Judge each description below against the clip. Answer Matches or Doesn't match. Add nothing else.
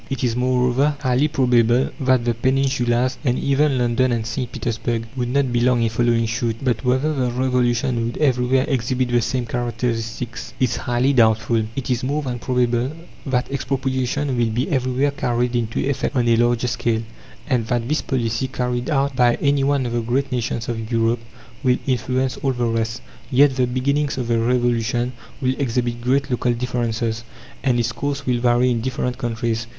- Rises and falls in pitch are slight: Matches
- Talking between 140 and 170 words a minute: Doesn't match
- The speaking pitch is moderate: Doesn't match